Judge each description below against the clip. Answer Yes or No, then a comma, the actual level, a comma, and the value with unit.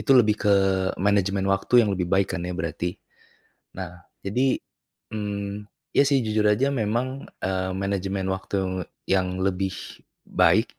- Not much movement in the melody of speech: Yes, narrow, 2.2 semitones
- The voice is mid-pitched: No, low, 100 Hz